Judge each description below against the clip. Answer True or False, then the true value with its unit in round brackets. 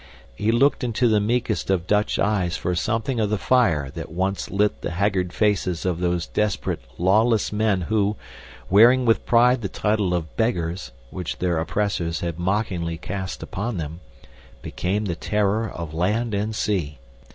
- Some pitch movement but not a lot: True (3.7 semitones)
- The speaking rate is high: False (165 wpm)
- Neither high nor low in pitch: False (100 Hz)